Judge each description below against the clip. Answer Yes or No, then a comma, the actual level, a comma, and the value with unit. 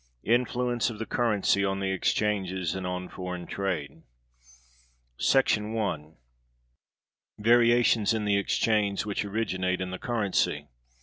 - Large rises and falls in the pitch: No, average, 3.3 semitones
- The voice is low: Yes, low, 100 Hz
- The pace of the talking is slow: Yes, slow, 120 wpm